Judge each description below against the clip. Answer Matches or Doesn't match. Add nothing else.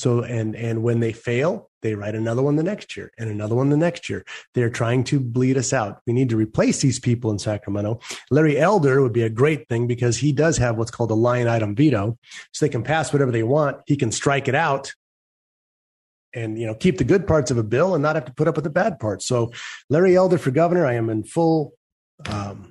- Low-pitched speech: Matches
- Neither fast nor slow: Doesn't match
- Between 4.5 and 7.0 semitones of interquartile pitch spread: Matches